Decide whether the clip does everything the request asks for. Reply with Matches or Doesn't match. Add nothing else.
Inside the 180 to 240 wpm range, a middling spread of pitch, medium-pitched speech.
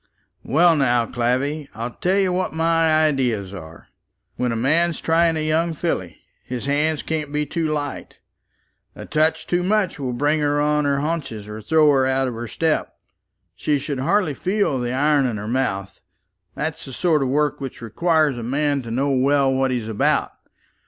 Matches